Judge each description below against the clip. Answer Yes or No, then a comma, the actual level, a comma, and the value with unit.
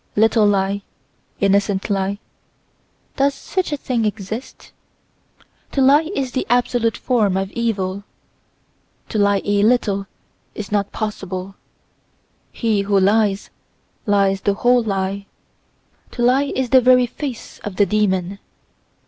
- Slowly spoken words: Yes, slow, 125 wpm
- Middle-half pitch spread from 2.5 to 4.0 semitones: Yes, average, 3.6 semitones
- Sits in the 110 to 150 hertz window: No, high, 210 Hz